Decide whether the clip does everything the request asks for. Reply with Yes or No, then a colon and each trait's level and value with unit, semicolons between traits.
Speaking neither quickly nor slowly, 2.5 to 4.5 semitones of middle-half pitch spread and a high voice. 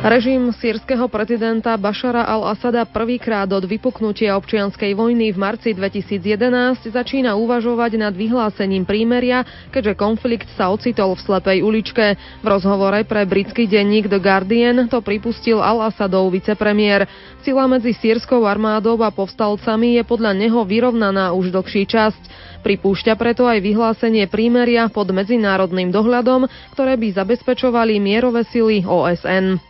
Yes: average, 125 wpm; average, 2.9 semitones; high, 220 Hz